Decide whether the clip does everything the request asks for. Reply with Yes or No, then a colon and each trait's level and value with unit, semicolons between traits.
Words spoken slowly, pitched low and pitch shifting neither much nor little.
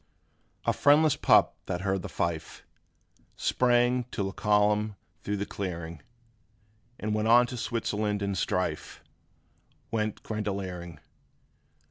Yes: slow, 110 wpm; low, 105 Hz; average, 3.5 semitones